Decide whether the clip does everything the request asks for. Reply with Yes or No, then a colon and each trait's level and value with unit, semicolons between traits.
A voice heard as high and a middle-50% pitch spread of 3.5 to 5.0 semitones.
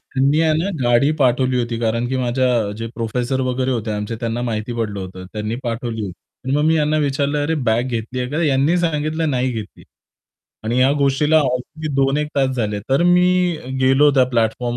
No: low, 130 Hz; average, 3.8 semitones